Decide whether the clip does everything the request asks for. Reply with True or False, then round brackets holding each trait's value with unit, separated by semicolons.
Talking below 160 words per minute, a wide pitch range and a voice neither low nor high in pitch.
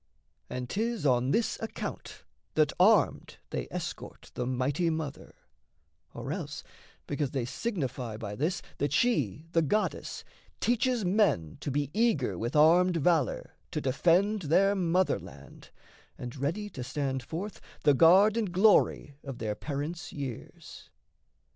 True (135 wpm; 6.7 semitones; 155 Hz)